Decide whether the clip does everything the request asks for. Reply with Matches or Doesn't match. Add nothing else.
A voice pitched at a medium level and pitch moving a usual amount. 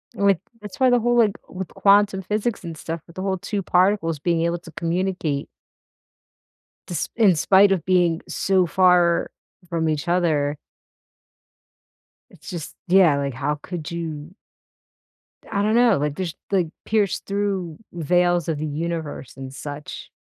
Matches